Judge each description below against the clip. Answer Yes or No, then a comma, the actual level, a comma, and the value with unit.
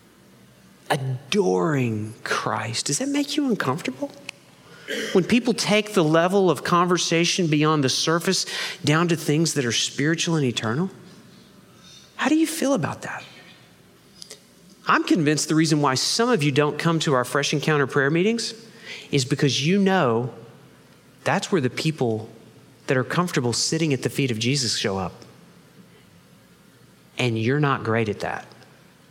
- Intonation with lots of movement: Yes, wide, 6.7 semitones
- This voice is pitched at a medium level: Yes, medium, 155 Hz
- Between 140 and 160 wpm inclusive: Yes, average, 150 wpm